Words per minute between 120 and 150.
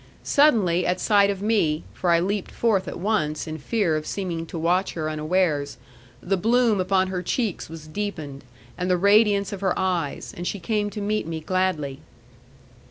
No: average, 180 wpm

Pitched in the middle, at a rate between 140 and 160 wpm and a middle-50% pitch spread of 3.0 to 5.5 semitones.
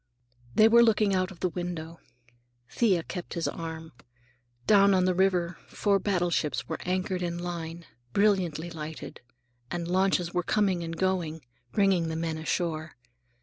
No: medium, 175 Hz; average, 145 wpm; narrow, 2.4 semitones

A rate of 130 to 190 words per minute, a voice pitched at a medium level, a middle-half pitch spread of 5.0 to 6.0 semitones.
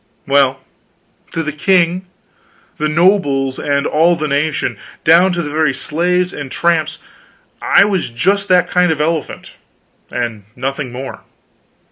No: average, 140 wpm; medium, 155 Hz; average, 4.2 semitones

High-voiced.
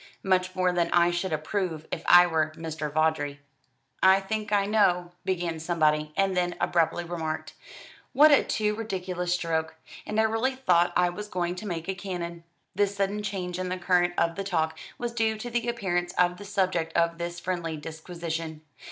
No: medium, 180 Hz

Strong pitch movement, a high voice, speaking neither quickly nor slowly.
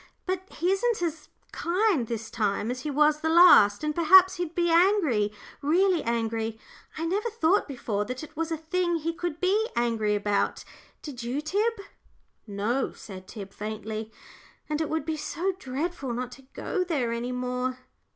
Yes: wide, 6.9 semitones; very high, 300 Hz; average, 170 wpm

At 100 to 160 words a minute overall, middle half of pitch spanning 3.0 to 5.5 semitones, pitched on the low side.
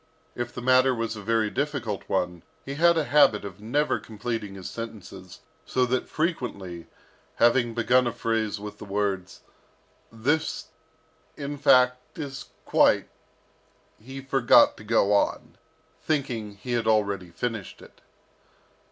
Yes: average, 140 wpm; average, 4.0 semitones; low, 115 Hz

